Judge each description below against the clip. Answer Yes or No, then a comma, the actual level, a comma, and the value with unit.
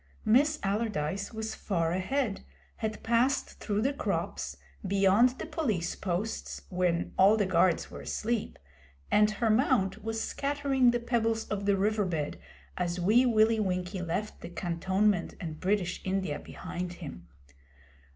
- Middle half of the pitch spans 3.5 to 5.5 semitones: Yes, average, 3.8 semitones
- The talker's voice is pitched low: No, high, 205 Hz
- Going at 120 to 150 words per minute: Yes, average, 140 wpm